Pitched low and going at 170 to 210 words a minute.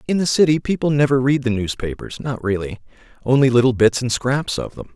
Yes: low, 130 Hz; fast, 205 wpm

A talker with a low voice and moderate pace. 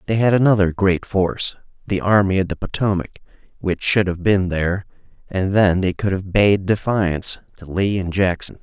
Yes: very low, 95 Hz; average, 180 wpm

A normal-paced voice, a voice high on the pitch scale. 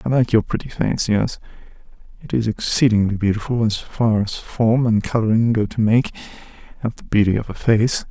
No: average, 185 wpm; low, 110 Hz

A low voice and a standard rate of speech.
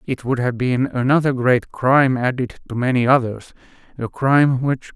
Yes: low, 130 Hz; average, 155 wpm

